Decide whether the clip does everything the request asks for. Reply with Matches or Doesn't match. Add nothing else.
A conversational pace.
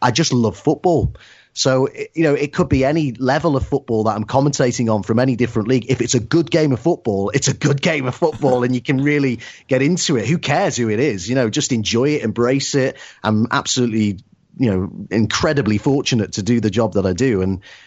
Doesn't match